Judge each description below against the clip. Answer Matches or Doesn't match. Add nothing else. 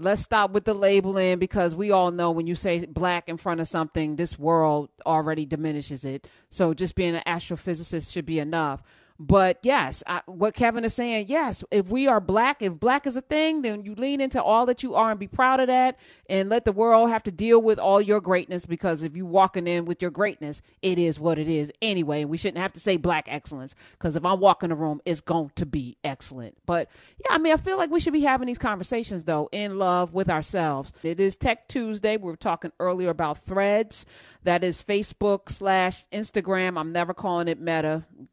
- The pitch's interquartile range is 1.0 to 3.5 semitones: Doesn't match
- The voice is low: Doesn't match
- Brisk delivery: Matches